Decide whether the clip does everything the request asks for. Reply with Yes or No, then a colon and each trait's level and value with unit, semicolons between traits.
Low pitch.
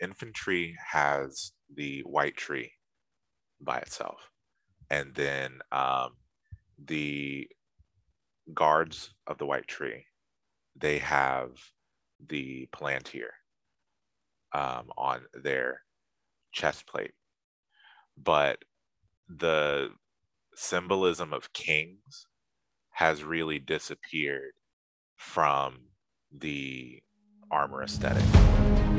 Yes: very low, 75 Hz